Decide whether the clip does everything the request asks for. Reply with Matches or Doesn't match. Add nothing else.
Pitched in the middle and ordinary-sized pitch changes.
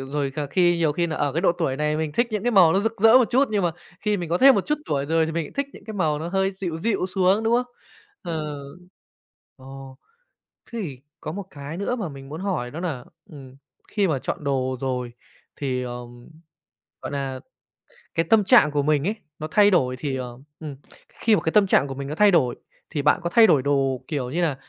Doesn't match